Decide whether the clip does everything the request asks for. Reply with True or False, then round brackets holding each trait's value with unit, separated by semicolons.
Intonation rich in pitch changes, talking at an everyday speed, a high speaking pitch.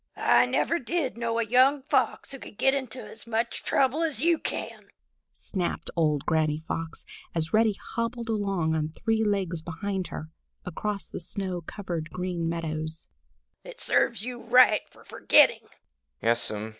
True (6.3 semitones; 150 wpm; 205 Hz)